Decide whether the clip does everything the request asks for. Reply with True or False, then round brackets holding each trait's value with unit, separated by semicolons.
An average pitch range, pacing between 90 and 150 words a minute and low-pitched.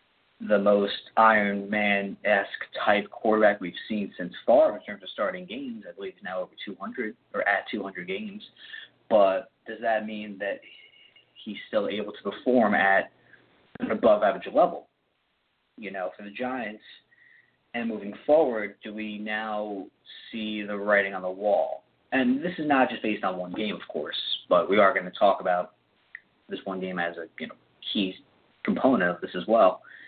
False (4.1 semitones; 180 wpm; 105 Hz)